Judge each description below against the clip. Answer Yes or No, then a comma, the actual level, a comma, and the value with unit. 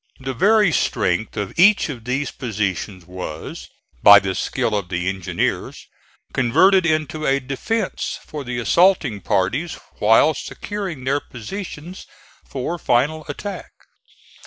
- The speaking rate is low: Yes, slow, 125 wpm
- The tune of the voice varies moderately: No, wide, 8.1 semitones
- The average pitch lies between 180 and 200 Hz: No, low, 135 Hz